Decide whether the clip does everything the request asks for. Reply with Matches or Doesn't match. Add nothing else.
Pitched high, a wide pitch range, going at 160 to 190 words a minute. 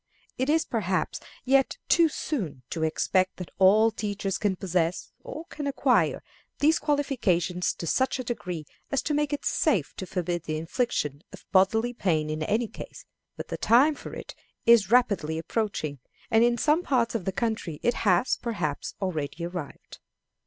Matches